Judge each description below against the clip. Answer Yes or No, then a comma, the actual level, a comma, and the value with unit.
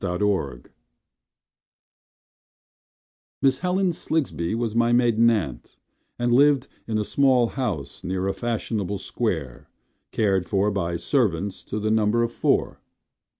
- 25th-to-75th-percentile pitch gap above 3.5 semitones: Yes, average, 4.0 semitones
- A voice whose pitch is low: Yes, low, 110 Hz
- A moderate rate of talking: No, slow, 125 wpm